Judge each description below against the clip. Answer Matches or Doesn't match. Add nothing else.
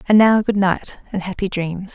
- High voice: Matches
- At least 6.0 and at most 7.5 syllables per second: Doesn't match